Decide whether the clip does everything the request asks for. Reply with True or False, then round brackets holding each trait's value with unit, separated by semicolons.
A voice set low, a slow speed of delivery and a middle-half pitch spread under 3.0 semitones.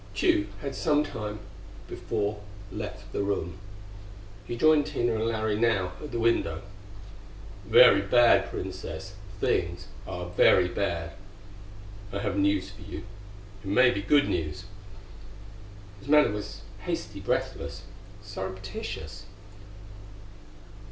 False (100 Hz; 115 wpm; 3.7 semitones)